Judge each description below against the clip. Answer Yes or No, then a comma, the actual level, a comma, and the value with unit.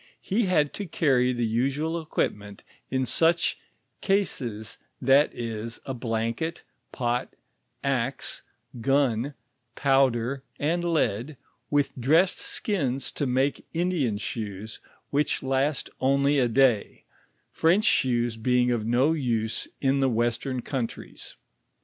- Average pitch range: Yes, average, 3.8 semitones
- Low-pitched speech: Yes, low, 130 Hz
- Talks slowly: Yes, slow, 115 wpm